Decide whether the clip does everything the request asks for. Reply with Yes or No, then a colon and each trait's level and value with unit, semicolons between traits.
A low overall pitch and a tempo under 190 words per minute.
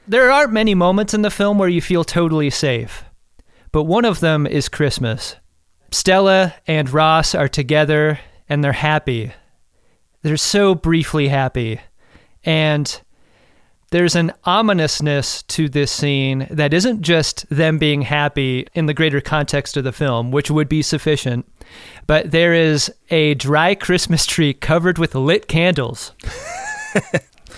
No: medium, 155 Hz; average, 140 wpm